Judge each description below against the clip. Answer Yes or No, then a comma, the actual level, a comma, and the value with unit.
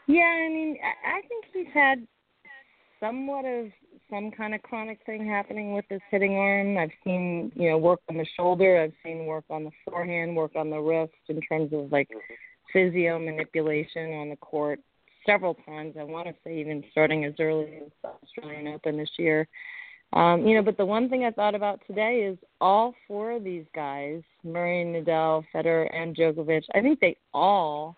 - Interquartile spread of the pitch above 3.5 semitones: Yes, average, 5.3 semitones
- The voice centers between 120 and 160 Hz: No, medium, 175 Hz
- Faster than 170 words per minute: Yes, average, 185 wpm